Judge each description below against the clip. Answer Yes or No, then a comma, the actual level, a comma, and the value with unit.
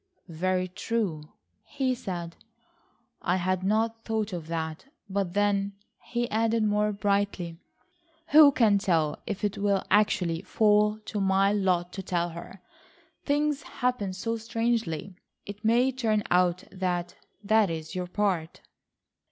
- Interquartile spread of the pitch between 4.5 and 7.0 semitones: No, average, 3.6 semitones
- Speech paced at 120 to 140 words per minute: Yes, slow, 135 wpm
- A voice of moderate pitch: No, high, 200 Hz